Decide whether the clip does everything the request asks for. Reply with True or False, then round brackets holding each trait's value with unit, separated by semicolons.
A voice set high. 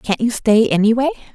True (230 Hz)